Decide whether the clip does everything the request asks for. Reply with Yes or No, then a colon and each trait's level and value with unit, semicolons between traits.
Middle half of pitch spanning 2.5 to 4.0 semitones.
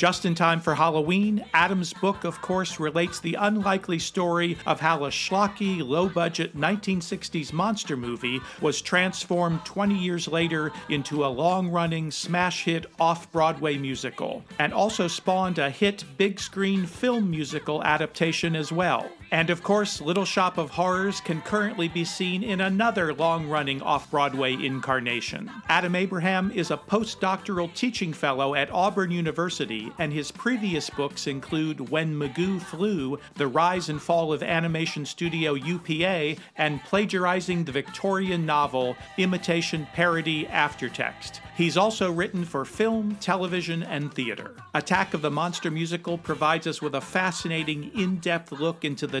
Yes: average, 3.5 semitones